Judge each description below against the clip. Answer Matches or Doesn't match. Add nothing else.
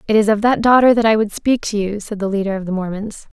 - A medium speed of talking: Doesn't match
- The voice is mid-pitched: Doesn't match